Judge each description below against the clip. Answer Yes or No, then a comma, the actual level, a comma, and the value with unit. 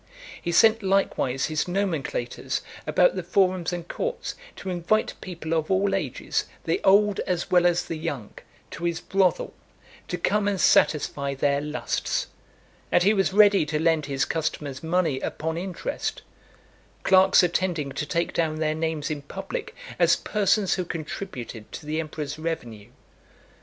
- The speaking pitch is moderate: Yes, medium, 170 Hz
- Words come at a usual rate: Yes, average, 150 wpm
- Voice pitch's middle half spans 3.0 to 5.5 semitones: Yes, average, 4.0 semitones